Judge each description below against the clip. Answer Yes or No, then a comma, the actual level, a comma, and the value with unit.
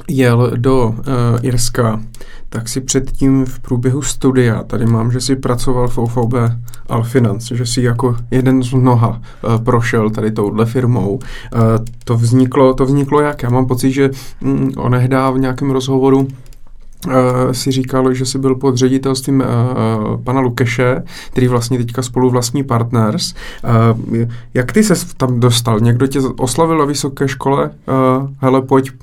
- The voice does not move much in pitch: Yes, narrow, 2.0 semitones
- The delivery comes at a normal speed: Yes, average, 160 wpm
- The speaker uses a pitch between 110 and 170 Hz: Yes, low, 125 Hz